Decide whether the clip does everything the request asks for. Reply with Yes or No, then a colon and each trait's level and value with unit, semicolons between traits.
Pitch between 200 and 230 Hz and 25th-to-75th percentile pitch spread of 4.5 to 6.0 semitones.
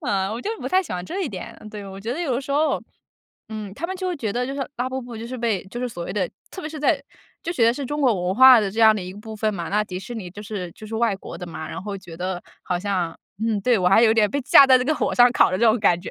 Yes: high, 220 Hz; average, 5.0 semitones